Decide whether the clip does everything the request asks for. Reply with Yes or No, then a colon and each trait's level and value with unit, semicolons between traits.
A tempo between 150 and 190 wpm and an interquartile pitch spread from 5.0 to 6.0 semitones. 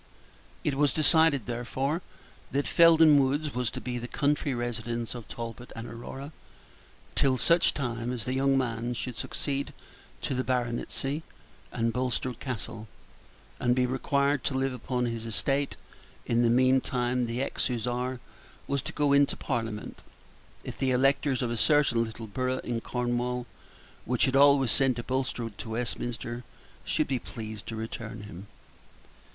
No: average, 155 wpm; narrow, 2.6 semitones